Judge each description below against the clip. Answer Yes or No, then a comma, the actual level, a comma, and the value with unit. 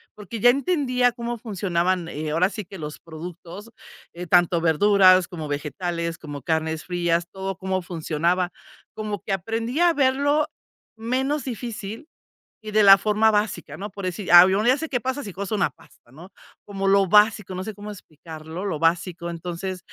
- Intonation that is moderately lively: Yes, average, 4.3 semitones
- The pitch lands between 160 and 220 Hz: Yes, high, 190 Hz